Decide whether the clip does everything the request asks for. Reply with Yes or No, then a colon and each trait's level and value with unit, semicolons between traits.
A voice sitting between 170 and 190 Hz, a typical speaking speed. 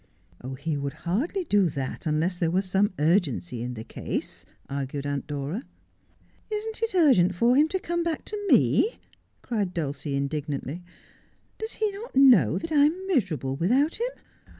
Yes: medium, 185 Hz; average, 175 wpm